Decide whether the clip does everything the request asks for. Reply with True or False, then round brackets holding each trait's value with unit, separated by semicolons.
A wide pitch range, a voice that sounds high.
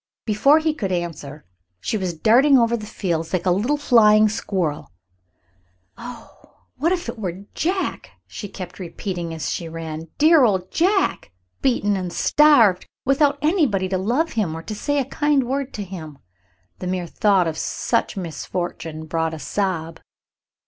True (7.5 semitones; 200 Hz)